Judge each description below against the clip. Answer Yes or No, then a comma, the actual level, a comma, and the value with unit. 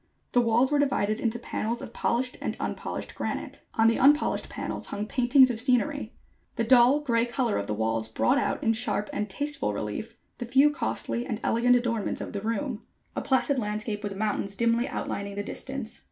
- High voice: Yes, high, 235 Hz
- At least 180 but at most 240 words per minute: Yes, average, 190 wpm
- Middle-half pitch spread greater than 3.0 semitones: Yes, average, 3.4 semitones